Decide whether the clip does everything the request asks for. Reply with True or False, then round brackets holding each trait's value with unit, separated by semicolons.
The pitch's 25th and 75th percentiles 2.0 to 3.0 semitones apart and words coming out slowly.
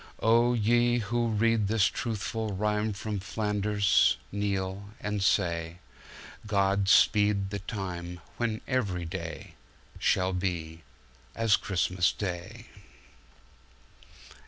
True (2.7 semitones; 85 wpm)